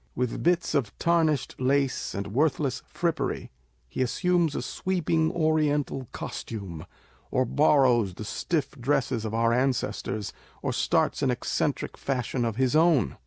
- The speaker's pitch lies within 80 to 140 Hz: Yes, low, 135 Hz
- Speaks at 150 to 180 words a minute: No, slow, 135 wpm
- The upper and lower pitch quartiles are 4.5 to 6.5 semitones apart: Yes, average, 5.1 semitones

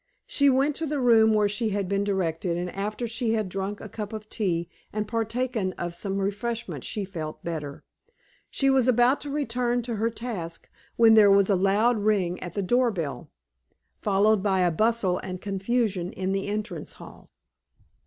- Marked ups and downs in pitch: No, average, 3.6 semitones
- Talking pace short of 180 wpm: No, average, 185 wpm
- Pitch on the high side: Yes, high, 210 Hz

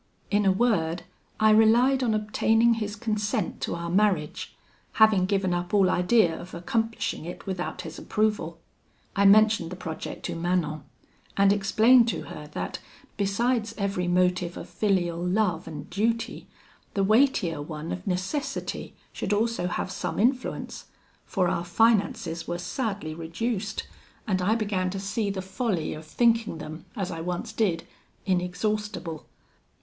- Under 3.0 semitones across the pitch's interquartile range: No, average, 3.7 semitones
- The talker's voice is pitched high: Yes, high, 195 Hz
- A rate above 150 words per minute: No, average, 145 wpm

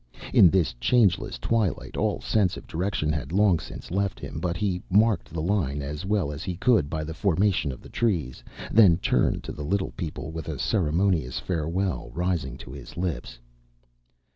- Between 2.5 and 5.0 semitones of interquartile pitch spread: Yes, average, 4.6 semitones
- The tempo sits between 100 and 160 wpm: No, average, 180 wpm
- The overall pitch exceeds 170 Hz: No, very low, 85 Hz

